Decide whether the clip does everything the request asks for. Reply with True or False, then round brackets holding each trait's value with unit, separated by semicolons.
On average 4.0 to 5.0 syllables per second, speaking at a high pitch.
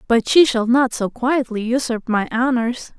True (4.4 syllables/s; 240 Hz)